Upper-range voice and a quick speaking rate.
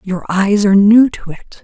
Yes: high, 200 Hz; fast, 220 wpm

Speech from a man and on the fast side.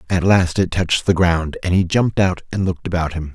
Yes: male; fast, 250 wpm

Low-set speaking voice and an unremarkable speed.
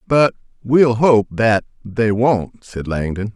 Yes: low, 115 Hz; average, 145 wpm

